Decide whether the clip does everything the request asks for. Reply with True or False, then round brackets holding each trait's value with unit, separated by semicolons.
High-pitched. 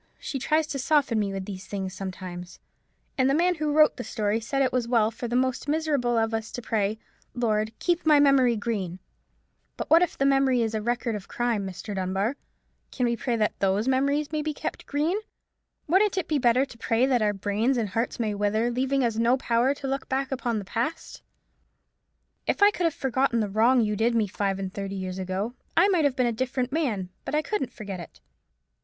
True (240 Hz)